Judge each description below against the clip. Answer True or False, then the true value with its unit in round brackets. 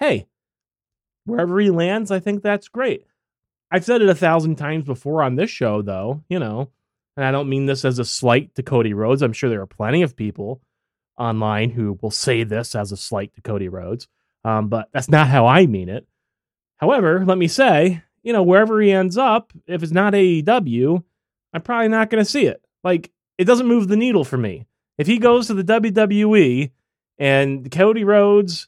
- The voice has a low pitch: False (155 Hz)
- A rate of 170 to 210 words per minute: True (200 wpm)